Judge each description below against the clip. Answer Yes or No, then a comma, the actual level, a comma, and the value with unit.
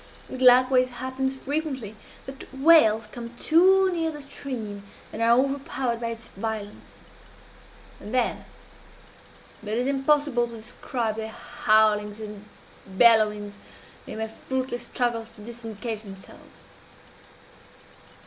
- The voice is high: Yes, high, 235 Hz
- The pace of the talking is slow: Yes, slow, 115 wpm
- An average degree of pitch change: Yes, average, 3.4 semitones